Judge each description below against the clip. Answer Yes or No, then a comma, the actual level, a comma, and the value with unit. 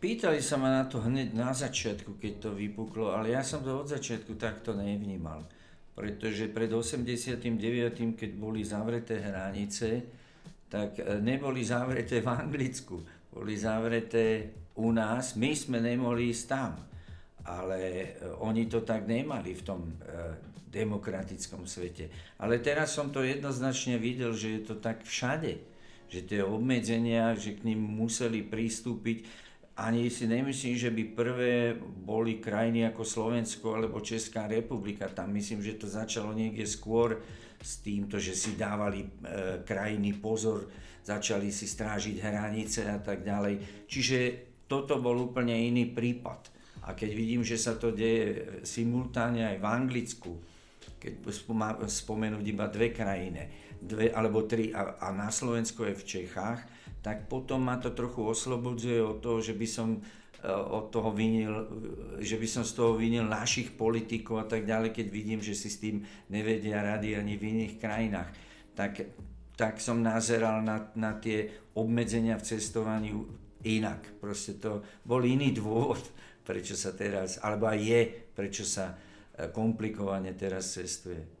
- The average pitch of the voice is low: Yes, low, 110 Hz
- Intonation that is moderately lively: No, narrow, 2.1 semitones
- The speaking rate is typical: Yes, average, 145 wpm